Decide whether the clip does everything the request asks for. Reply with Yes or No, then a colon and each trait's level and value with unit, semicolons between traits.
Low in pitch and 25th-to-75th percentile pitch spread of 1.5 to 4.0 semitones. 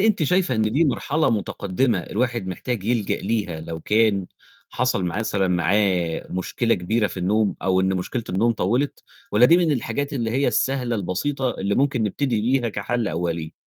No: low, 110 Hz; average, 5.2 semitones